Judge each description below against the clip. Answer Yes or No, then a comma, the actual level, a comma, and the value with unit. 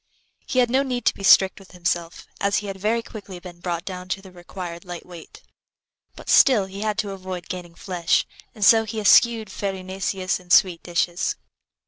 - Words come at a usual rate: Yes, average, 190 wpm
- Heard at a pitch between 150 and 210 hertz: Yes, high, 190 Hz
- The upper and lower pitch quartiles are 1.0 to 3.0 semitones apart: Yes, average, 2.7 semitones